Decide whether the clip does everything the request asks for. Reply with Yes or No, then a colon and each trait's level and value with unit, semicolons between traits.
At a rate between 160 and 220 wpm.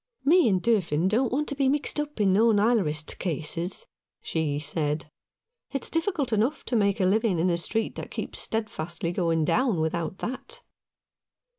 Yes: average, 170 wpm